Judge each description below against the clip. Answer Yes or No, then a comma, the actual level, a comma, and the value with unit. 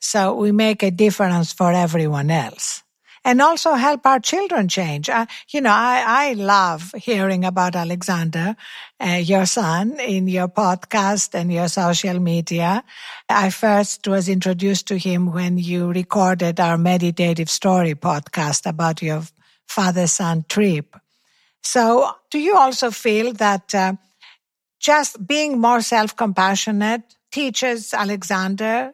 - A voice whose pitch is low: No, high, 195 Hz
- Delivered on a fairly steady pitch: No, average, 4.5 semitones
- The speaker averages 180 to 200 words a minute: No, slow, 135 wpm